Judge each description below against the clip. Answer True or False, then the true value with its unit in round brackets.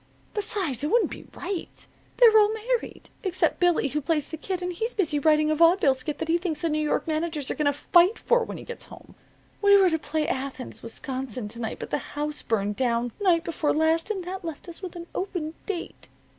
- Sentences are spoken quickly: True (225 wpm)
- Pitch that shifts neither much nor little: True (4.2 semitones)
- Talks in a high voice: True (325 Hz)